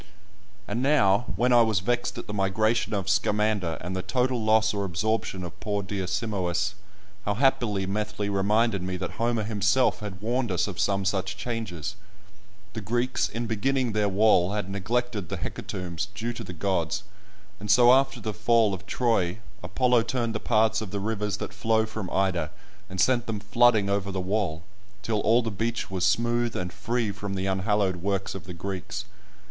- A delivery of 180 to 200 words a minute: Yes, average, 185 wpm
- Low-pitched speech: Yes, low, 105 Hz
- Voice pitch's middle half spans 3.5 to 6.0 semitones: No, average, 3.0 semitones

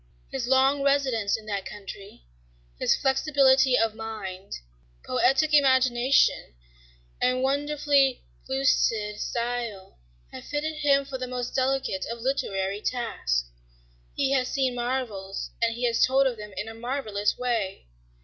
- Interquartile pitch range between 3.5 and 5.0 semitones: Yes, average, 4.0 semitones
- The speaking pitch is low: No, very high, 250 Hz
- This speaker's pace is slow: Yes, slow, 130 wpm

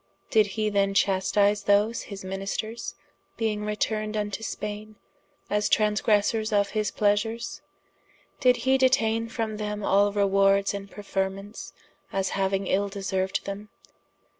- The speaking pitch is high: Yes, high, 205 Hz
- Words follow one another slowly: Yes, slow, 125 wpm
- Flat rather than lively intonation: Yes, narrow, 1.6 semitones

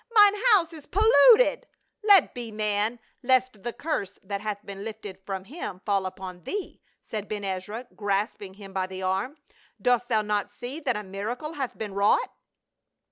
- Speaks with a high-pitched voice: Yes, high, 215 Hz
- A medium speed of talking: Yes, average, 190 wpm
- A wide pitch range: No, average, 4.8 semitones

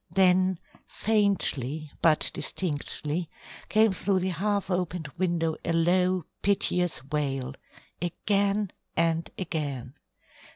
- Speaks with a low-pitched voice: No, medium, 175 Hz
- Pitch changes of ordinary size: Yes, average, 3.4 semitones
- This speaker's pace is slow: Yes, slow, 95 wpm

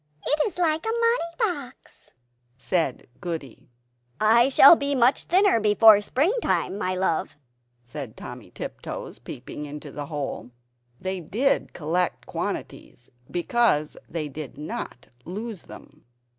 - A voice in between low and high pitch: No, high, 200 Hz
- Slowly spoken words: Yes, slow, 125 wpm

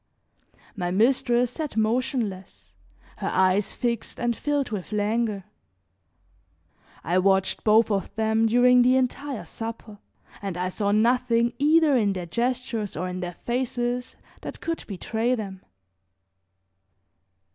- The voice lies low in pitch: No, high, 225 Hz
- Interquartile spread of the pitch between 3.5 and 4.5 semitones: Yes, average, 3.9 semitones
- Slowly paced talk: Yes, slow, 125 wpm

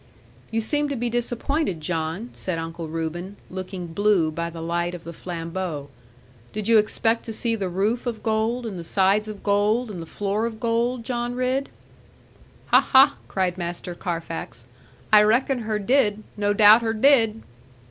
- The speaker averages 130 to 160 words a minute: No, average, 170 wpm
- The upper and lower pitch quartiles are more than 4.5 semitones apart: Yes, average, 5.0 semitones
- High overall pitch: Yes, high, 210 Hz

